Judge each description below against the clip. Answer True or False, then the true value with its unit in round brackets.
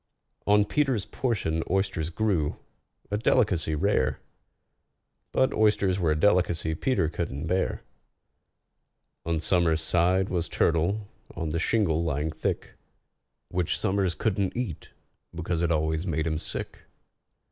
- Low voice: True (90 Hz)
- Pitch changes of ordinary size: True (4.0 semitones)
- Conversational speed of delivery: False (120 wpm)